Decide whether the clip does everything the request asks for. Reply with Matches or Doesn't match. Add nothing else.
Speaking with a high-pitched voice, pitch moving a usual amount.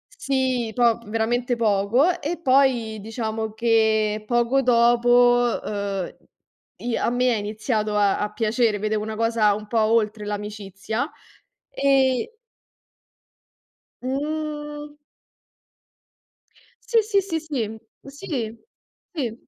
Matches